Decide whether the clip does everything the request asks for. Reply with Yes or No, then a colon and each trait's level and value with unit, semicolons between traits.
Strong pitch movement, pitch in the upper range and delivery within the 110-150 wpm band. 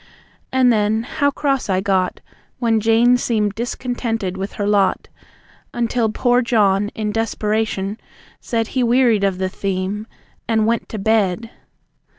No: average, 2.8 semitones; high, 220 Hz; average, 140 wpm